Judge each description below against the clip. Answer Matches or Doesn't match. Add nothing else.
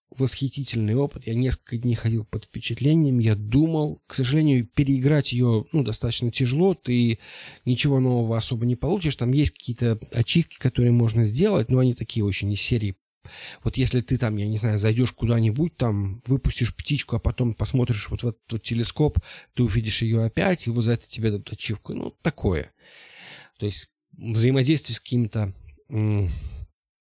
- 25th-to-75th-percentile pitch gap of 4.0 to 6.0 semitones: Doesn't match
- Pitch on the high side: Doesn't match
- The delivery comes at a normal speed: Doesn't match